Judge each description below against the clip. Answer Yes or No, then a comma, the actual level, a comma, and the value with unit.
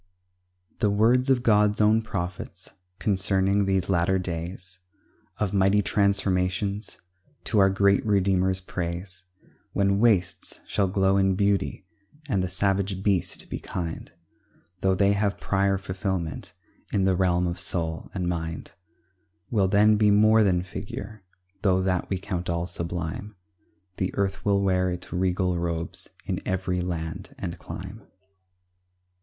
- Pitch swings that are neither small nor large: No, narrow, 1.8 semitones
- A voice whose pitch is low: Yes, very low, 95 Hz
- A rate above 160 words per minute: No, slow, 135 wpm